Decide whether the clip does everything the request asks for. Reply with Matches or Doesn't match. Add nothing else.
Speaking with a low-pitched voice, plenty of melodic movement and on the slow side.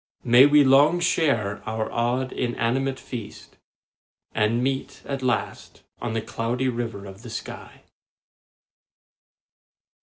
Doesn't match